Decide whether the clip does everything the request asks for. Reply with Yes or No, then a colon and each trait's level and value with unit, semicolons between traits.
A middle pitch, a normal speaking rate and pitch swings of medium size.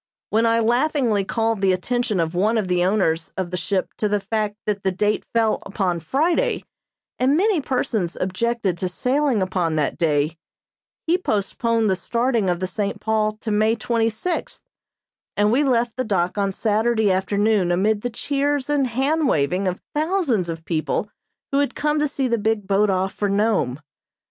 No: high, 215 Hz; average, 180 wpm; average, 4.5 semitones